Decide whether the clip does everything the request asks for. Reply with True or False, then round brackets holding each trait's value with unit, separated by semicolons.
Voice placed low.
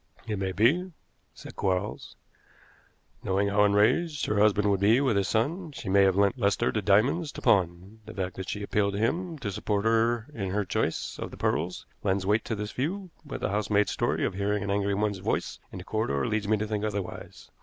True (105 Hz)